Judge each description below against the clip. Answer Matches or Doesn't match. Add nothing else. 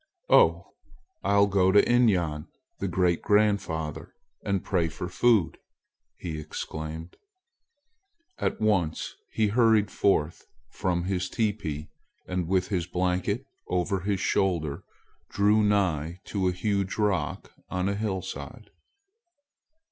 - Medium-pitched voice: Doesn't match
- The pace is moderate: Doesn't match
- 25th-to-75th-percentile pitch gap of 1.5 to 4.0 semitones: Matches